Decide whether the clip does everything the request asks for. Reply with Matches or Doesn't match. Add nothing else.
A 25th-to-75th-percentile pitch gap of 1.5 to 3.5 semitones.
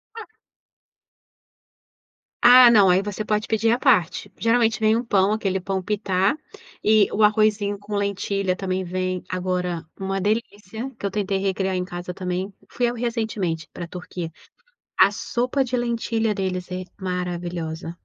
Matches